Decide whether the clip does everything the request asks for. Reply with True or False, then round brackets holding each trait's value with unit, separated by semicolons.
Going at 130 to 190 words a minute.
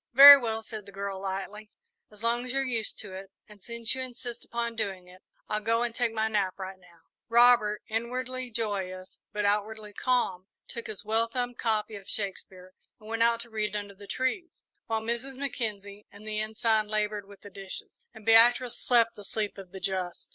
False (200 wpm)